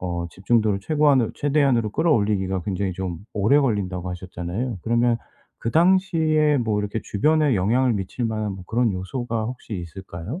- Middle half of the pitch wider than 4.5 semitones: Yes, wide, 5.6 semitones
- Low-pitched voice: Yes, low, 110 Hz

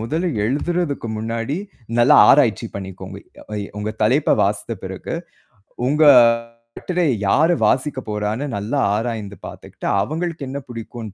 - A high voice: No, low, 120 Hz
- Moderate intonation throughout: No, wide, 5.8 semitones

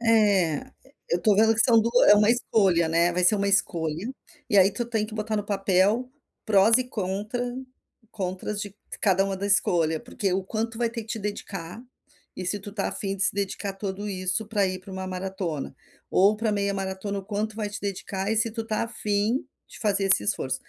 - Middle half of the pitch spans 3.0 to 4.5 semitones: No, narrow, 2.4 semitones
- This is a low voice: No, high, 200 Hz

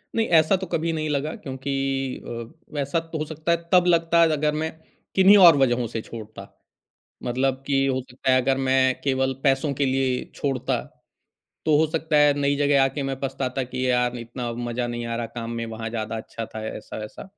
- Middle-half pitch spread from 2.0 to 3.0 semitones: No, average, 4.0 semitones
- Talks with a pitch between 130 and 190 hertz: Yes, low, 135 Hz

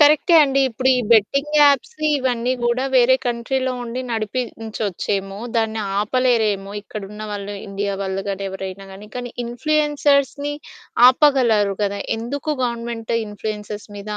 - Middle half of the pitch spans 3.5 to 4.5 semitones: Yes, average, 4.0 semitones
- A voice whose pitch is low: No, high, 230 Hz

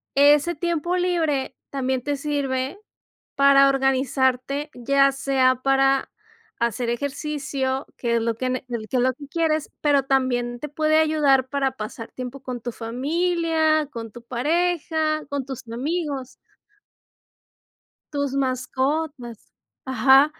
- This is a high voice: Yes, very high, 275 Hz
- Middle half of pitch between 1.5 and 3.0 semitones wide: Yes, average, 2.7 semitones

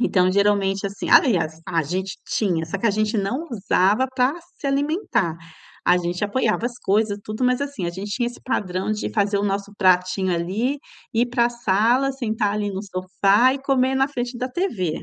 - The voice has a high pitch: Yes, high, 210 Hz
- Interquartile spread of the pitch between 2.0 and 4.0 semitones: No, average, 4.7 semitones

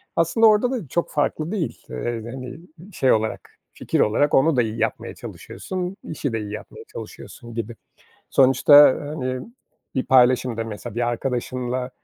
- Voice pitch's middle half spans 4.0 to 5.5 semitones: Yes, average, 4.3 semitones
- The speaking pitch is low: Yes, low, 130 Hz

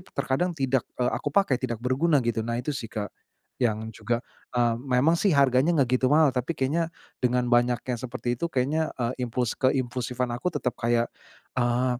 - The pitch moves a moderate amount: No, narrow, 2.3 semitones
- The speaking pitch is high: No, low, 125 Hz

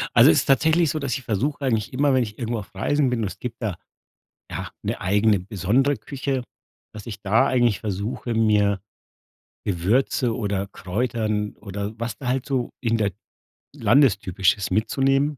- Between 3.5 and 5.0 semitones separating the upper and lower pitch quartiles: Yes, average, 4.4 semitones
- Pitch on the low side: Yes, low, 115 Hz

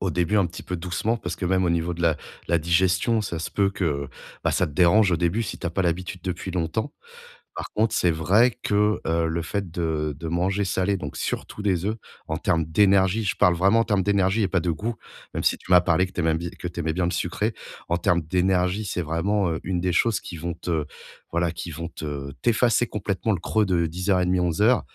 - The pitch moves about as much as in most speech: Yes, average, 3.0 semitones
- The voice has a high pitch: No, very low, 90 Hz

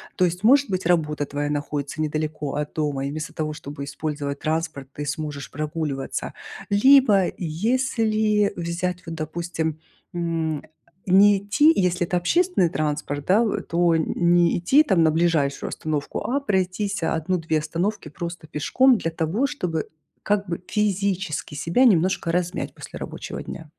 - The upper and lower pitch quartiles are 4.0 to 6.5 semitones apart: Yes, average, 4.5 semitones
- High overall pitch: No, medium, 170 Hz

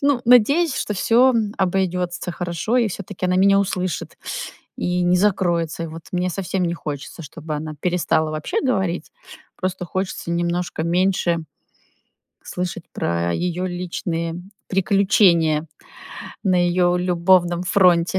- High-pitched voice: No, medium, 180 Hz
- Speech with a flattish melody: Yes, narrow, 2.1 semitones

